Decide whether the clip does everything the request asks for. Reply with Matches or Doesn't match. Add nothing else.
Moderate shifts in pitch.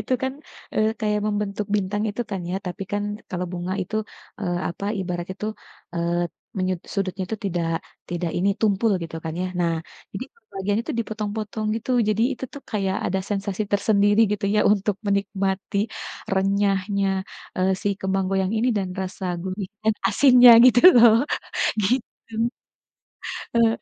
Doesn't match